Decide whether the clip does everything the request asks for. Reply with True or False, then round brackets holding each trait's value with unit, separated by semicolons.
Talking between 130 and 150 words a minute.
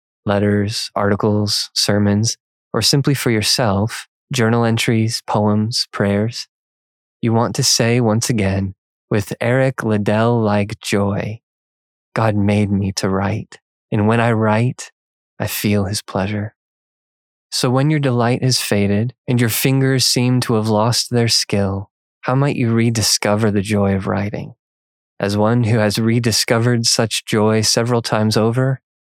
True (140 wpm)